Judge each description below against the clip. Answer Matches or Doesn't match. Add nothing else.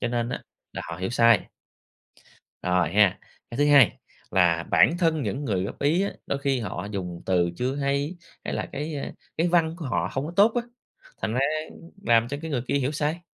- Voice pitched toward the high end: Doesn't match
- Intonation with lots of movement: Matches